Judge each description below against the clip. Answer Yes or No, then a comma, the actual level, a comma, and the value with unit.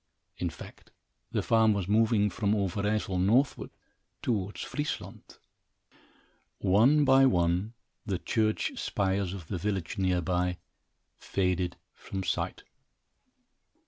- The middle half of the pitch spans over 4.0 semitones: No, average, 3.2 semitones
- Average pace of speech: No, slow, 110 wpm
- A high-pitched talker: No, low, 100 Hz